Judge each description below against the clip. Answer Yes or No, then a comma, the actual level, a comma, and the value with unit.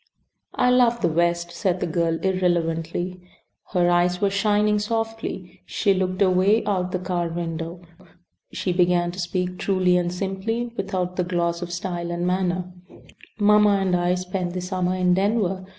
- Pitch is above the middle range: No, medium, 180 Hz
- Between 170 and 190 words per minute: No, average, 160 wpm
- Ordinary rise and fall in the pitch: No, narrow, 1.8 semitones